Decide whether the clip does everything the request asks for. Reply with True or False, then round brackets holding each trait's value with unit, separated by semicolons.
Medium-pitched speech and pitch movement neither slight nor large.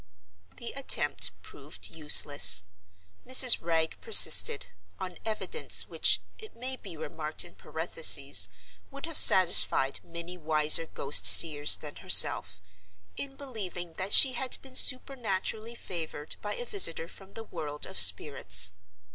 False (175 Hz; 7.7 semitones)